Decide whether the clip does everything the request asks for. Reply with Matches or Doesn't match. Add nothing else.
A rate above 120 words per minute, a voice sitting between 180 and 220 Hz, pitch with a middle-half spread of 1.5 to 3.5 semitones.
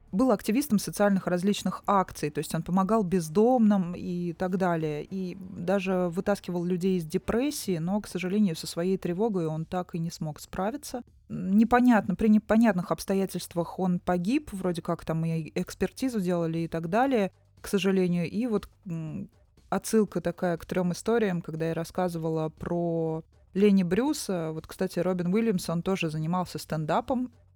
Matches